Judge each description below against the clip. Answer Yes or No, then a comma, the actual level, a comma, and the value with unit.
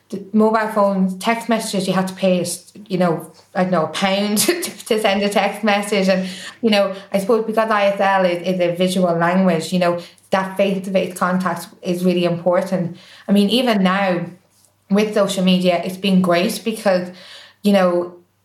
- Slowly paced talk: No, average, 185 wpm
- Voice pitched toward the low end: No, high, 190 Hz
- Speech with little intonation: Yes, narrow, 2.1 semitones